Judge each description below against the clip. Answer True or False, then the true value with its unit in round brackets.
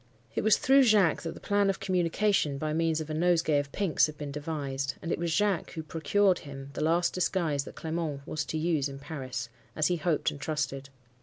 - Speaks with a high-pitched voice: False (155 Hz)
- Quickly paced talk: True (215 wpm)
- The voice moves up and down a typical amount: True (3.6 semitones)